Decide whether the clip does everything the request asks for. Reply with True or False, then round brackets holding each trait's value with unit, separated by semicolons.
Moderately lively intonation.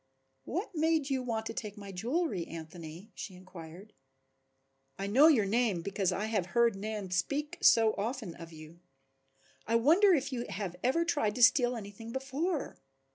False (5.7 semitones)